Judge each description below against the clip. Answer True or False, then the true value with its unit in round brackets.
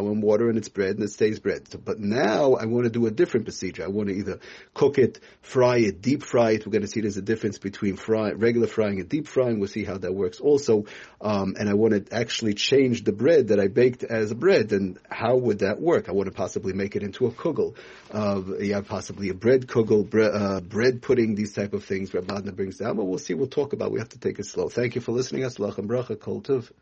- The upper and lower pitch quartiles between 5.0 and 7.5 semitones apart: False (2.9 semitones)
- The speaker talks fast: True (255 wpm)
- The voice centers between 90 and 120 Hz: True (105 Hz)